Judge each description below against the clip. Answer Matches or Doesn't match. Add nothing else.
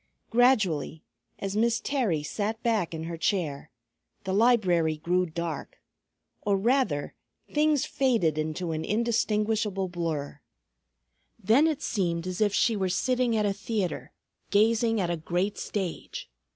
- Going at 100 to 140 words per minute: Matches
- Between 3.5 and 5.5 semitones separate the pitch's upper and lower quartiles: Matches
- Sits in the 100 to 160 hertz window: Doesn't match